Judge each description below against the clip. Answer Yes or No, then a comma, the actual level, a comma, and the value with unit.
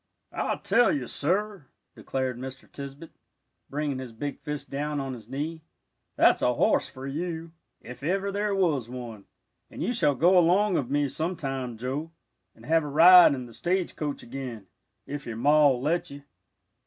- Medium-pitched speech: Yes, medium, 145 Hz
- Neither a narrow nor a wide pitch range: Yes, average, 4.2 semitones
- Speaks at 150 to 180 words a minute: Yes, average, 170 wpm